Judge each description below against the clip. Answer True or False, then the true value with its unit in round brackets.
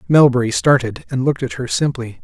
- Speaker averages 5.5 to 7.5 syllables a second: True (5.9 syllables/s)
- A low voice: True (125 Hz)